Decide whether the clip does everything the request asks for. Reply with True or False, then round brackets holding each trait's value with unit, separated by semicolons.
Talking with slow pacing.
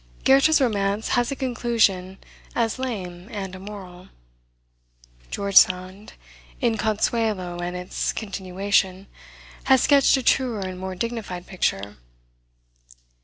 True (110 wpm)